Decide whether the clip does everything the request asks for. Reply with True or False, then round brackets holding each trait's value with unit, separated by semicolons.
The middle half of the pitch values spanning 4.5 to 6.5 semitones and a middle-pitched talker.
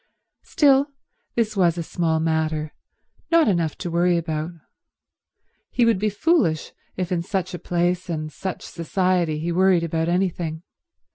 False (2.7 semitones; 175 Hz)